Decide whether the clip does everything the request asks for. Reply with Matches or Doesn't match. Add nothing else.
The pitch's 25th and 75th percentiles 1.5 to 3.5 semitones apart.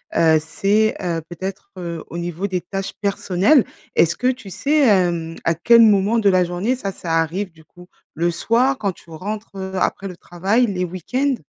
Doesn't match